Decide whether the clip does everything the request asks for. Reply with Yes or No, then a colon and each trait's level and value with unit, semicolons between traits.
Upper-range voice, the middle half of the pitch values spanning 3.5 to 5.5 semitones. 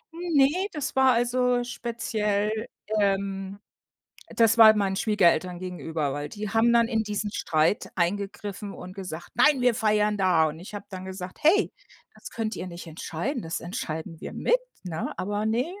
Yes: high, 205 Hz; average, 4.2 semitones